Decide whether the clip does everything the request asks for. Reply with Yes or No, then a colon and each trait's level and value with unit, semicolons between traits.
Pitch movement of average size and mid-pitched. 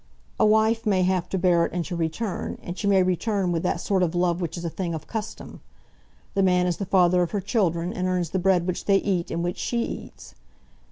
No: narrow, 2.1 semitones; medium, 180 Hz